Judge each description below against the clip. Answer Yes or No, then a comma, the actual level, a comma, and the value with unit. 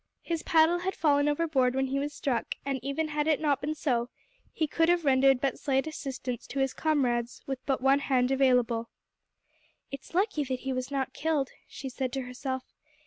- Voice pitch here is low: No, very high, 275 Hz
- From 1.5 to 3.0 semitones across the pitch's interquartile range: Yes, average, 2.7 semitones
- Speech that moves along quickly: No, average, 195 wpm